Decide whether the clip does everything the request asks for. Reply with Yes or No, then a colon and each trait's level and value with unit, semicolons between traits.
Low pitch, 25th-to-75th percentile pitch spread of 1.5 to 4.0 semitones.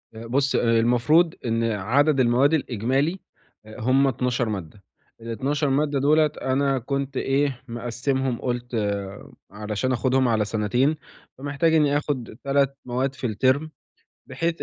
Yes: low, 130 Hz; average, 3.2 semitones